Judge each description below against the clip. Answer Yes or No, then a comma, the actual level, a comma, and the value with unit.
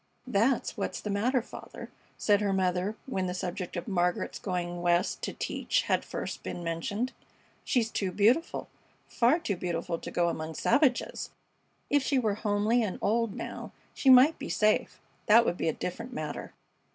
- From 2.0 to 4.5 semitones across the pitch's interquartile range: No, average, 5.0 semitones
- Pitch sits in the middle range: No, high, 205 Hz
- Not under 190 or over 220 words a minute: No, average, 170 wpm